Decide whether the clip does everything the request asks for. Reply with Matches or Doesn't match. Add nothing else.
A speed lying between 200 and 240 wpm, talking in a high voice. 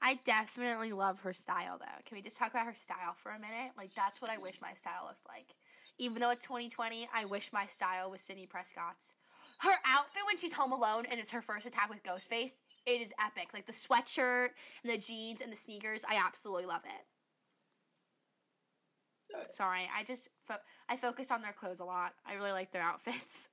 Matches